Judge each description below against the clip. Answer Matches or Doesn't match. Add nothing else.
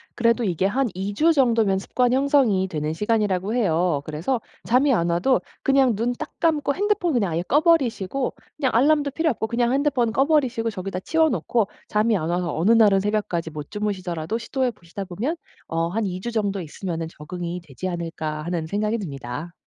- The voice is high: Matches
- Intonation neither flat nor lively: Doesn't match